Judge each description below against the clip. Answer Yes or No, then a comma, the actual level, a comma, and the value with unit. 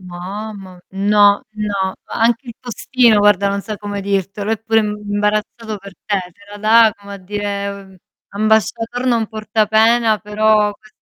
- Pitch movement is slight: Yes, narrow, 1.5 semitones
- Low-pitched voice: No, high, 210 Hz